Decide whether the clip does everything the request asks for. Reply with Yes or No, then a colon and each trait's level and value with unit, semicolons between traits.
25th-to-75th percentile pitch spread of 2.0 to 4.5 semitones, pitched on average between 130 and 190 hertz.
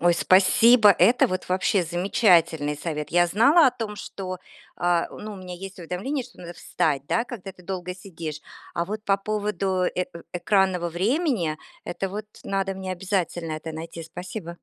Yes: average, 3.3 semitones; medium, 185 Hz